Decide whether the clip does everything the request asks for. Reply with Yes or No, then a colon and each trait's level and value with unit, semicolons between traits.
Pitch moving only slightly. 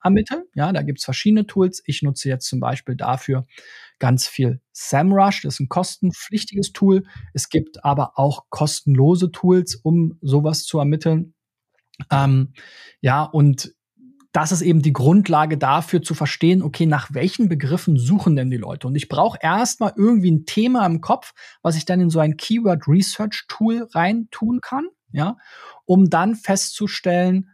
No: wide, 5.4 semitones